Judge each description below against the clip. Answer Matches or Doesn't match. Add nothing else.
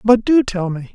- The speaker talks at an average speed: Doesn't match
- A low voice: Doesn't match